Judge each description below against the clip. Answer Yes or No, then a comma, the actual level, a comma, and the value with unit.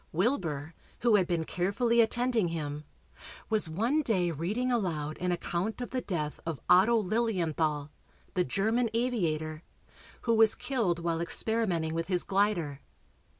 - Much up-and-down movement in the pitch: Yes, wide, 5.8 semitones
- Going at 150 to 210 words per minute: No, average, 140 wpm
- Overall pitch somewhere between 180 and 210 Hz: Yes, medium, 185 Hz